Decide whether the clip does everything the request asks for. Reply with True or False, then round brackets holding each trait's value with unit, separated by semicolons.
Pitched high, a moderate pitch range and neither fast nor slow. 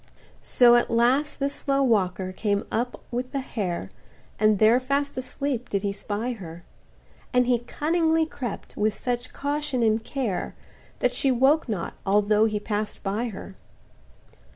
True (240 Hz; 4.4 semitones; 155 wpm)